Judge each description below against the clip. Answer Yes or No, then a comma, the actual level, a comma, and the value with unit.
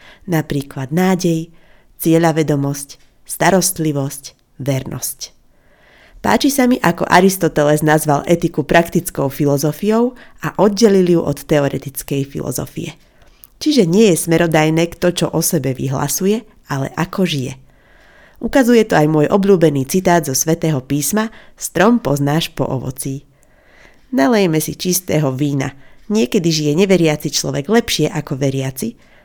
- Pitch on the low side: No, medium, 160 Hz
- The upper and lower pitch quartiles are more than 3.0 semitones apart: Yes, average, 4.5 semitones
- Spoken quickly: No, average, 115 wpm